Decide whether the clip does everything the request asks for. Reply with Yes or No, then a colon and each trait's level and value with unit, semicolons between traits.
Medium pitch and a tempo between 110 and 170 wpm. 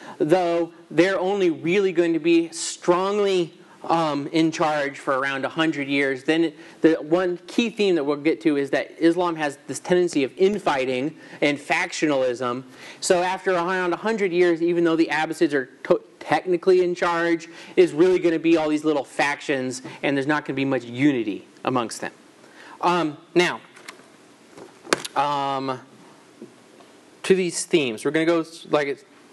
Yes: medium, 165 Hz; average, 160 wpm